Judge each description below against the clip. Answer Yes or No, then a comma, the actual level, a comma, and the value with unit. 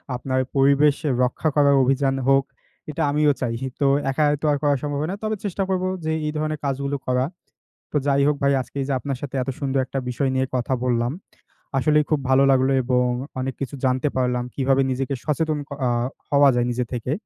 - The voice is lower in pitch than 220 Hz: Yes, low, 135 Hz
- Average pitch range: No, narrow, 2.1 semitones